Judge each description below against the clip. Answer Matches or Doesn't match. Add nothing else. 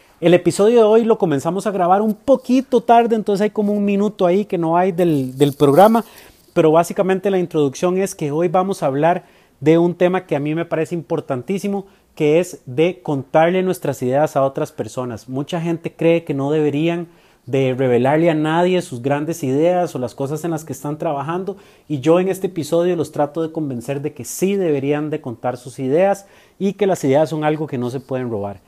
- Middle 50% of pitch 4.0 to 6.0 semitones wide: Matches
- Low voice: Doesn't match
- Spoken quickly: Matches